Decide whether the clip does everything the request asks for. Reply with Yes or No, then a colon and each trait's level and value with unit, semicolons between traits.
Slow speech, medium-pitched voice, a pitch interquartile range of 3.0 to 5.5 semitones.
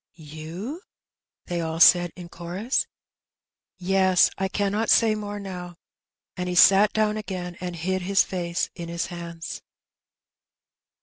No: slow, 130 wpm; medium, 180 Hz; narrow, 2.5 semitones